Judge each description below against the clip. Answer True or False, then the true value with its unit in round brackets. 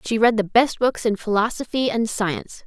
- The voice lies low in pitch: False (220 Hz)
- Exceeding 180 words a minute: True (200 wpm)